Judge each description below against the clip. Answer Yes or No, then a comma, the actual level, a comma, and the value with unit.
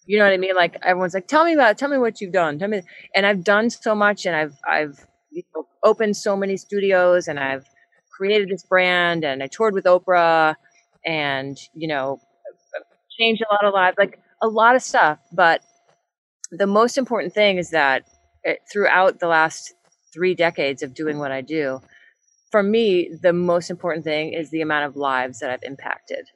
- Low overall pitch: No, medium, 185 Hz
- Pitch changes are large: No, average, 5.0 semitones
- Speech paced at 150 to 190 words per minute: No, fast, 205 wpm